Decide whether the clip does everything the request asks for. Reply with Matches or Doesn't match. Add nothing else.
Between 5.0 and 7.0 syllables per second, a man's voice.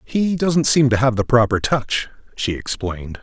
Doesn't match